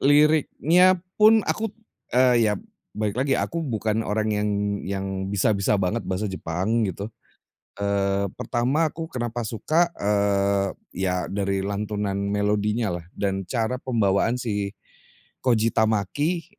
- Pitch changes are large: No, average, 4.3 semitones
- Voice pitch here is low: Yes, low, 105 Hz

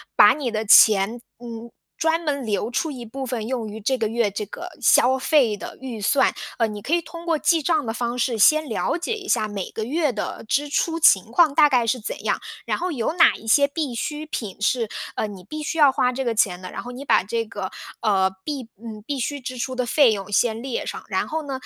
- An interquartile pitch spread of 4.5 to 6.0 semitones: Yes, average, 5.0 semitones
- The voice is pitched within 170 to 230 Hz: No, high, 245 Hz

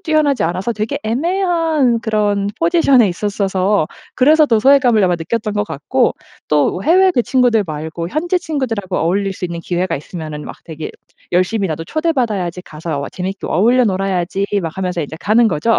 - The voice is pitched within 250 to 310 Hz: No, high, 205 Hz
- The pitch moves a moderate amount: No, wide, 6.4 semitones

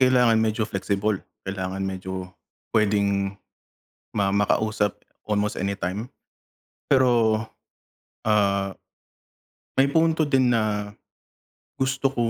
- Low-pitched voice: Yes, low, 105 Hz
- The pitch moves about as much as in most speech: Yes, average, 3.3 semitones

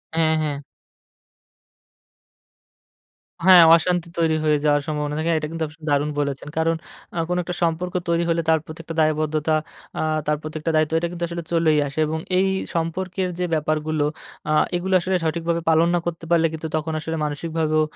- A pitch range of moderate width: No, narrow, 1.5 semitones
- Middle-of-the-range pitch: Yes, medium, 160 Hz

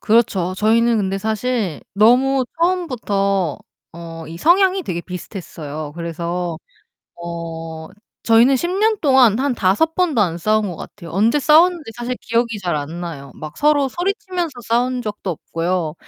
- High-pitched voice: Yes, high, 215 Hz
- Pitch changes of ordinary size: No, wide, 7.7 semitones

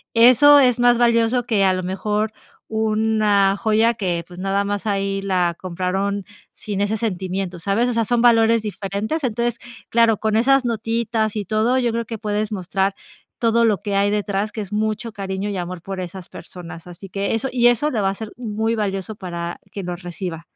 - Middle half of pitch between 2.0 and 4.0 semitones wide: Yes, average, 2.9 semitones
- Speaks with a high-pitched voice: Yes, high, 210 Hz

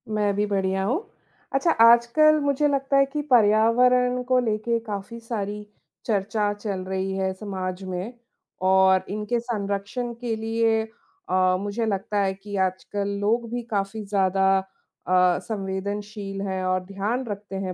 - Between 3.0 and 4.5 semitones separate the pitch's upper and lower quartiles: Yes, average, 3.3 semitones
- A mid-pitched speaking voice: No, high, 205 Hz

